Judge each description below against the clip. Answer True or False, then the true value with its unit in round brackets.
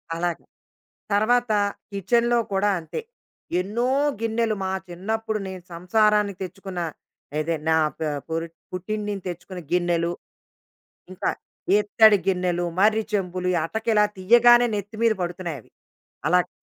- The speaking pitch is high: True (195 Hz)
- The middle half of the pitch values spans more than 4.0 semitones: False (3.6 semitones)